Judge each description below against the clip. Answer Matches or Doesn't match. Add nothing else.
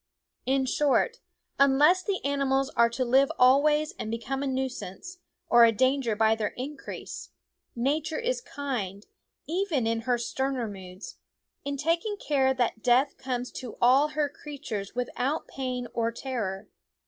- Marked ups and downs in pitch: Doesn't match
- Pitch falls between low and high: Doesn't match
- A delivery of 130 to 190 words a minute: Matches